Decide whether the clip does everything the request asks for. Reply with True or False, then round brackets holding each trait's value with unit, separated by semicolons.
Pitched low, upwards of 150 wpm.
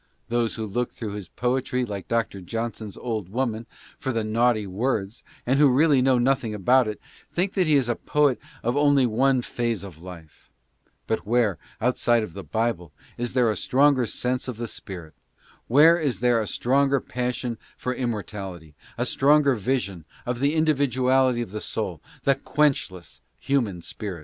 True (120 Hz; 160 wpm)